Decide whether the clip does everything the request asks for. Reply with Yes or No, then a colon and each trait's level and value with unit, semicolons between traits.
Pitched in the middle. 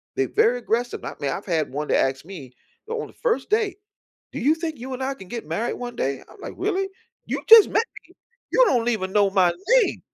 No: high, 240 Hz